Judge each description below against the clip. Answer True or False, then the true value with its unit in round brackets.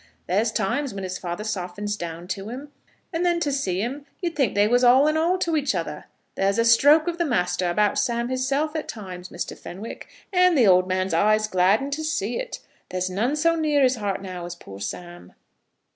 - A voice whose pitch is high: True (220 Hz)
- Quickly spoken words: True (210 wpm)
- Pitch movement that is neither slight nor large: False (7.7 semitones)